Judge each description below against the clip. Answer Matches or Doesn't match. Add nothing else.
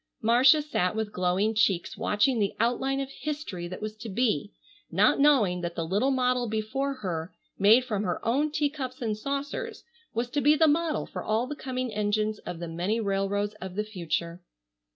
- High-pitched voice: Matches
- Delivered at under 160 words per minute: Doesn't match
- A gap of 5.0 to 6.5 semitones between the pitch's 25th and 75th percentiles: Matches